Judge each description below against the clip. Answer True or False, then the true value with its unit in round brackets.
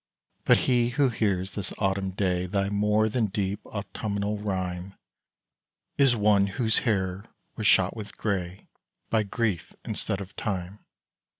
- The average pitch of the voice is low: True (100 Hz)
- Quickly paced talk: False (135 wpm)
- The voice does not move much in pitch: True (2.2 semitones)